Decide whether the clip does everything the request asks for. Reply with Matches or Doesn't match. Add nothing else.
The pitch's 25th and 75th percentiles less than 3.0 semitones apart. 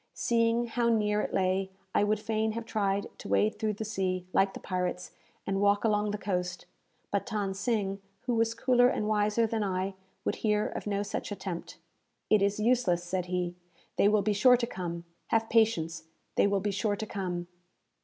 Matches